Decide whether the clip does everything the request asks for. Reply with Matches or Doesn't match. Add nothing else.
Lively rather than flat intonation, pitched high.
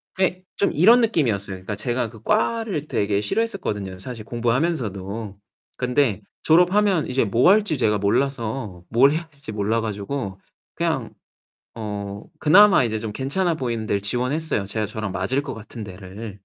Doesn't match